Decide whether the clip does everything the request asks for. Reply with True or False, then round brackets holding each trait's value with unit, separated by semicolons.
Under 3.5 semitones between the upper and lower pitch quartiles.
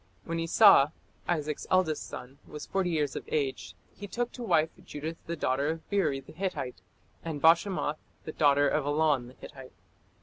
True (3.0 semitones)